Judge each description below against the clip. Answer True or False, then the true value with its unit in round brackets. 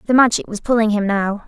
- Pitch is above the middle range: True (215 Hz)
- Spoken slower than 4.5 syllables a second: False (6.1 syllables/s)